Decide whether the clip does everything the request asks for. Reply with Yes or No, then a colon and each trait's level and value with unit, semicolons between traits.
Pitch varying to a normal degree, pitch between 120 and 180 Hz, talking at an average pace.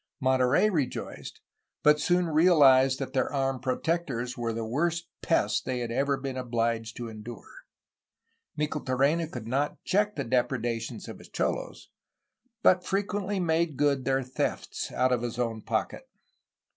Yes: average, 4.8 semitones; low, 135 Hz; average, 145 wpm